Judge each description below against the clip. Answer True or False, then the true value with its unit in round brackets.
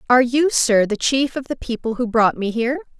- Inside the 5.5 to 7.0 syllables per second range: True (5.7 syllables/s)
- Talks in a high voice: True (245 Hz)